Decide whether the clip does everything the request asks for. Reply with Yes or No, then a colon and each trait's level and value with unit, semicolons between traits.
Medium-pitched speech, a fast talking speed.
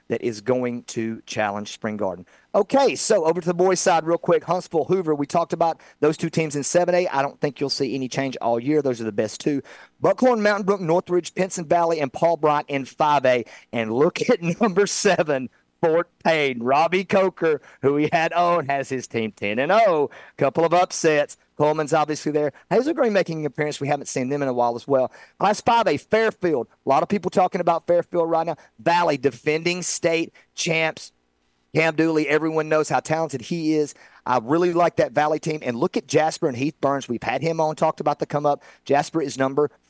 Yes: medium, 155 Hz; fast, 210 wpm